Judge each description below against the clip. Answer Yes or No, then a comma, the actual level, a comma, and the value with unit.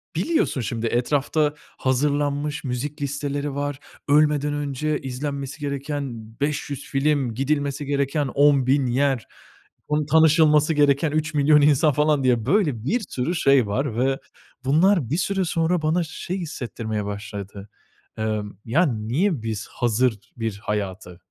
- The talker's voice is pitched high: No, medium, 140 Hz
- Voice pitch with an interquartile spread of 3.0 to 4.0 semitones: Yes, average, 3.3 semitones